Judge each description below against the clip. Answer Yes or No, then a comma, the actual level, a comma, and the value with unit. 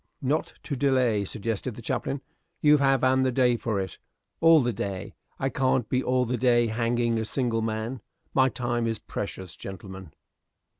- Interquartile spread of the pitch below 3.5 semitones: Yes, average, 3.0 semitones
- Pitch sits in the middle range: No, low, 120 Hz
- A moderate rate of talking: Yes, average, 170 wpm